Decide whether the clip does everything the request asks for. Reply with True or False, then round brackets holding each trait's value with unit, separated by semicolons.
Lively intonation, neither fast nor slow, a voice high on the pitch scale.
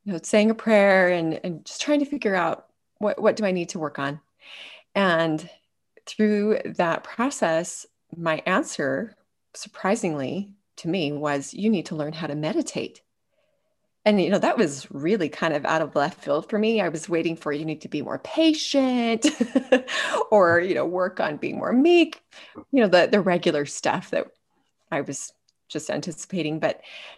True (6.5 semitones; 180 wpm; 195 Hz)